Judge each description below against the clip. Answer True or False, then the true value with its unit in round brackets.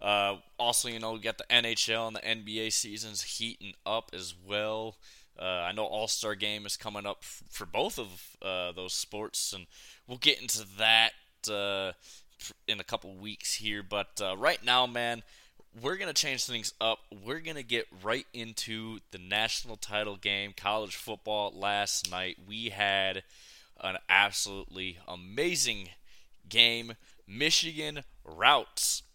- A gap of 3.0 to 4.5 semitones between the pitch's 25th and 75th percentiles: False (2.5 semitones)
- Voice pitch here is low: True (110 Hz)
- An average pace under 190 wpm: True (150 wpm)